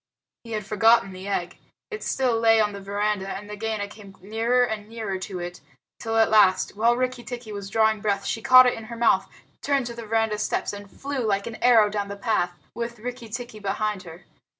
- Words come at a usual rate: No, fast, 215 wpm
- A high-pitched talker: Yes, high, 220 Hz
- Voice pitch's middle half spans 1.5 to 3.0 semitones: Yes, narrow, 2.5 semitones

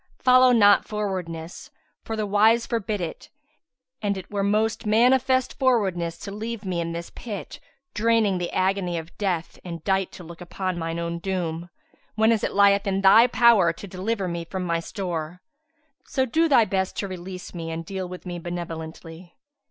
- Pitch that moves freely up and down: No, average, 3.8 semitones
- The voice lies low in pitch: No, high, 190 Hz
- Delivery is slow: No, average, 175 wpm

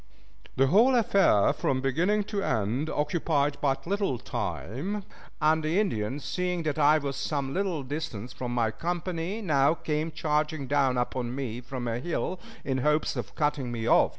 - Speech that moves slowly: No, average, 165 wpm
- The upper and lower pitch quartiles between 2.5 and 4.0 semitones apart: No, average, 4.6 semitones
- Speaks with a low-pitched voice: No, medium, 150 Hz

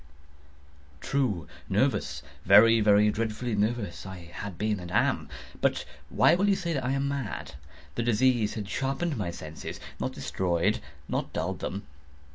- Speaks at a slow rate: Yes, slow, 130 wpm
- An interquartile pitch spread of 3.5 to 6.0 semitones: Yes, wide, 5.6 semitones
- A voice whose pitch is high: No, low, 105 Hz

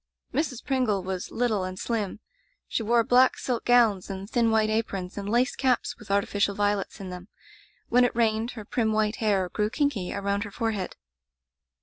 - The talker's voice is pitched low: No, high, 215 Hz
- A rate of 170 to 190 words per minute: Yes, average, 180 wpm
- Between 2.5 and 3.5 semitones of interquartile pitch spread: Yes, average, 3.0 semitones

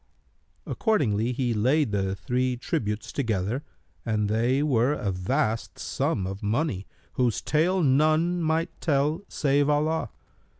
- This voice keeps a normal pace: No, slow, 130 wpm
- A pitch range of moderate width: No, wide, 6.1 semitones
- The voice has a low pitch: Yes, low, 130 Hz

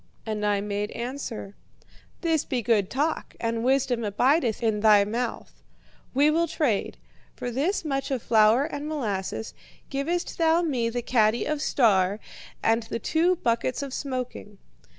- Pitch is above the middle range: Yes, high, 245 Hz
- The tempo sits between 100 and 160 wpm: Yes, average, 150 wpm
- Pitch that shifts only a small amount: No, average, 4.8 semitones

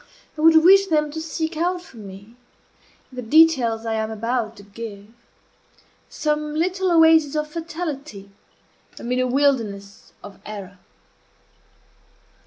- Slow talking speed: Yes, slow, 130 wpm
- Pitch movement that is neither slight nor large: No, wide, 6.6 semitones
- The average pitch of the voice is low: No, very high, 275 Hz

